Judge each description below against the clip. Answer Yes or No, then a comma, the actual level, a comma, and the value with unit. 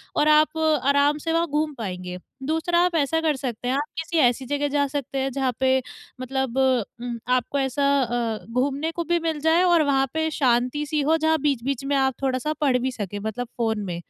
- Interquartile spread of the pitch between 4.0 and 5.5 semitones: No, average, 3.6 semitones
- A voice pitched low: No, very high, 275 Hz